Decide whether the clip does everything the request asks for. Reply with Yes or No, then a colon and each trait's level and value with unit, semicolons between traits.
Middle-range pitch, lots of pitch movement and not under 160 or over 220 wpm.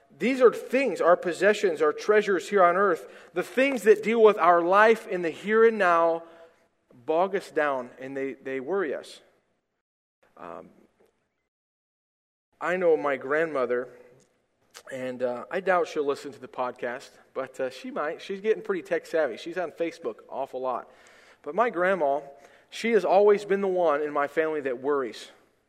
Yes: medium, 180 Hz; wide, 6.9 semitones; average, 170 wpm